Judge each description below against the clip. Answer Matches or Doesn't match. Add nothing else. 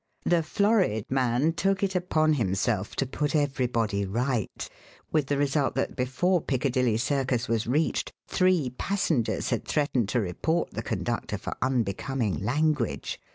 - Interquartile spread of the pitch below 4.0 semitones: Doesn't match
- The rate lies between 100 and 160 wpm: Matches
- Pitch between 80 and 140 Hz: Matches